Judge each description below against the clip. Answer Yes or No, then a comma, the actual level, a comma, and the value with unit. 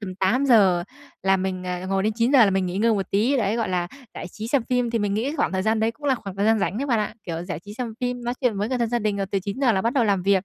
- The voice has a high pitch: Yes, high, 215 Hz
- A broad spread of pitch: No, average, 3.8 semitones